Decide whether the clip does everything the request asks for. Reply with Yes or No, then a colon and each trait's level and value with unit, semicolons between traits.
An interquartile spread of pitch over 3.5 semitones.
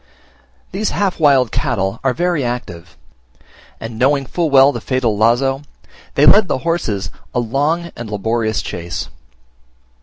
Yes: average, 4.9 semitones